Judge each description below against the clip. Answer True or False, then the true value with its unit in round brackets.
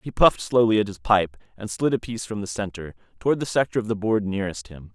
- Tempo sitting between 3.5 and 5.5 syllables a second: False (6.6 syllables/s)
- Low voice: True (105 Hz)